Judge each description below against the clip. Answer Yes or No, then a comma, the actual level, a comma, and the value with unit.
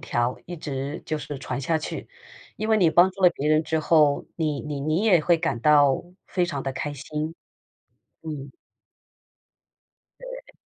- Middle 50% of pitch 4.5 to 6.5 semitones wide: No, average, 3.3 semitones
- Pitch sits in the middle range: Yes, medium, 155 Hz